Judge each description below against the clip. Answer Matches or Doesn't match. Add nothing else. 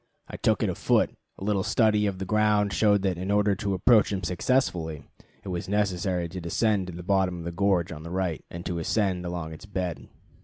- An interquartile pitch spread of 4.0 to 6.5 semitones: Doesn't match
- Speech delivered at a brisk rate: Matches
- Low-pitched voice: Matches